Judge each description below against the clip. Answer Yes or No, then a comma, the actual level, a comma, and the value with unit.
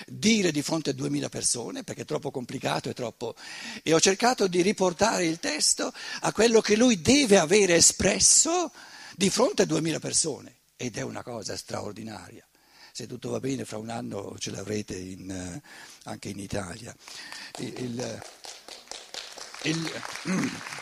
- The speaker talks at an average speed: Yes, average, 150 wpm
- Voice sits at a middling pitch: Yes, medium, 155 Hz